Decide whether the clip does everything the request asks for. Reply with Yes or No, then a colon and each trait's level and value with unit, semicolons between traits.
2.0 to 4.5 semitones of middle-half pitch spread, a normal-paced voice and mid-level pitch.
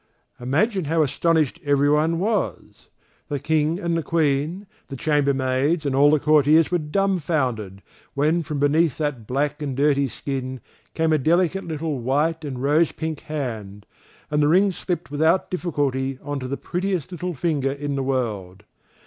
Yes: average, 3.3 semitones; average, 160 wpm; medium, 150 Hz